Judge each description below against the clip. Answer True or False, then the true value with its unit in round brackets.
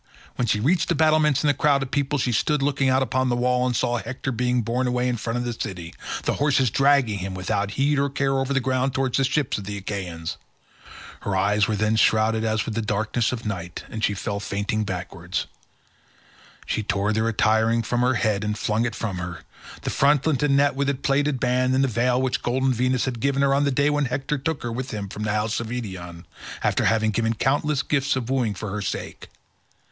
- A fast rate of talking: True (225 wpm)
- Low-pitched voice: True (120 Hz)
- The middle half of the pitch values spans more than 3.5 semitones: True (4.2 semitones)